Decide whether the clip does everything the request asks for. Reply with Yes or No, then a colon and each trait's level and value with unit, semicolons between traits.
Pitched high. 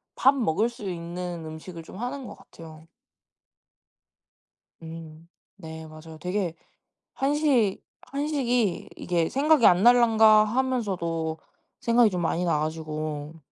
No: medium, 180 Hz